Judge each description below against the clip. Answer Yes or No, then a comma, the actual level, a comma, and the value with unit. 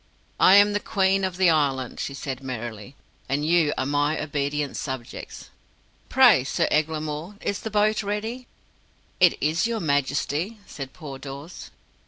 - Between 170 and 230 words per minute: No, average, 150 wpm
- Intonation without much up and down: No, wide, 5.6 semitones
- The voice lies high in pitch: No, medium, 155 Hz